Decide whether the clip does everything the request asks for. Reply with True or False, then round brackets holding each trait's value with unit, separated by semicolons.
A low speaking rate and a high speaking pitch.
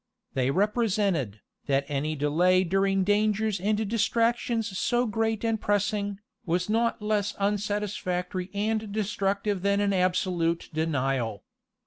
True (115 wpm; 200 Hz)